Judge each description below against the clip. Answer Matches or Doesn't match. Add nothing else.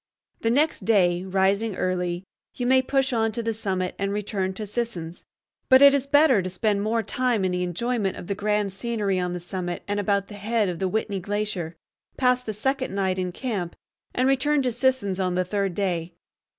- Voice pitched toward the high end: Matches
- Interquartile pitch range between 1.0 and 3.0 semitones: Doesn't match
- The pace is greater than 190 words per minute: Matches